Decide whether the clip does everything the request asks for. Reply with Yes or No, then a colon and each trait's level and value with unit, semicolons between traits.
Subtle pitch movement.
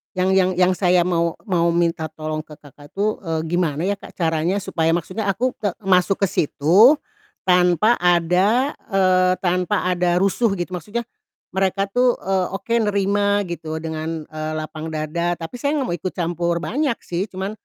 No: average, 3.0 semitones